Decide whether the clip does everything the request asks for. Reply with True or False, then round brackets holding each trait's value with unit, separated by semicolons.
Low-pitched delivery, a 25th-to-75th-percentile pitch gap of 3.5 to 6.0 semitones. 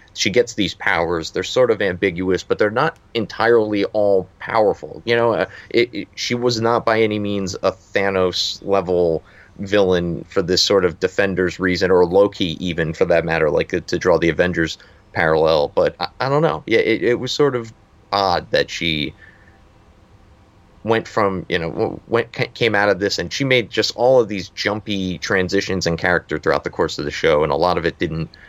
True (100 Hz; 4.4 semitones)